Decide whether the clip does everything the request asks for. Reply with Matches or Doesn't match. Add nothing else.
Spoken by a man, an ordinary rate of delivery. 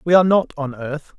Doesn't match